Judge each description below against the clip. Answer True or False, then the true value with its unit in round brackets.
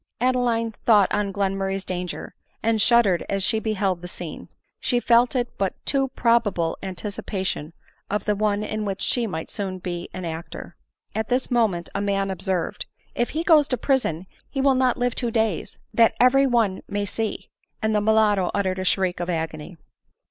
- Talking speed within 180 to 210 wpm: True (190 wpm)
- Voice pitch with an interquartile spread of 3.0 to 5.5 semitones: True (4.0 semitones)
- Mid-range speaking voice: False (205 Hz)